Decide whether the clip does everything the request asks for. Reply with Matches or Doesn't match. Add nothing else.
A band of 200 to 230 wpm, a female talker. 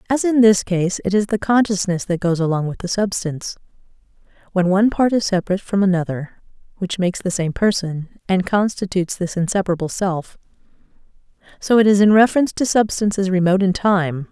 Doesn't match